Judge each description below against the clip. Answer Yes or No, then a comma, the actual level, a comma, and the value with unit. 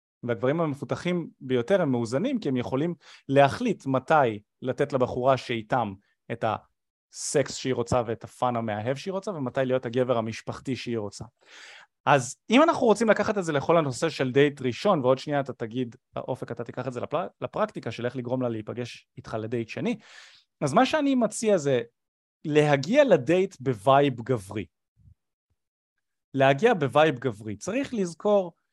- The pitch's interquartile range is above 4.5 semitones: Yes, wide, 5.5 semitones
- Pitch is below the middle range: Yes, low, 130 Hz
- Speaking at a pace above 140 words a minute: Yes, fast, 150 wpm